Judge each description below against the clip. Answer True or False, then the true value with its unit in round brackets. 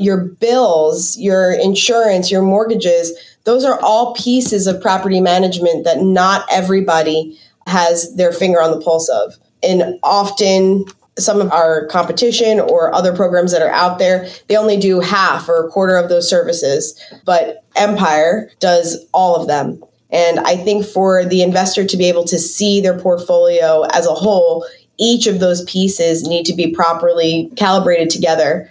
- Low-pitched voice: False (185 Hz)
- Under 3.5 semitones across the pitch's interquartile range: True (3.0 semitones)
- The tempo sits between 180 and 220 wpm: False (165 wpm)